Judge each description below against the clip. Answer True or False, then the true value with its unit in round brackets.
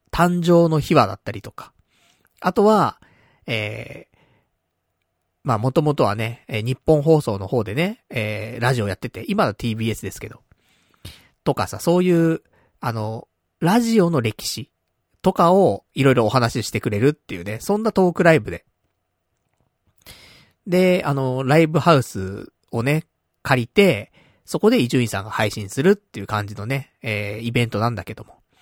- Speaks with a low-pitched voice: True (120 Hz)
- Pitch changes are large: True (7.2 semitones)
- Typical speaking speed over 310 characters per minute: False (305 characters per minute)